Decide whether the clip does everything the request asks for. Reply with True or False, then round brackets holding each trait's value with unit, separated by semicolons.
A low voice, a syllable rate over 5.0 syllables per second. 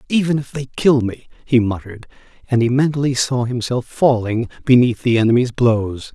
True (120 Hz; 5.3 syllables/s)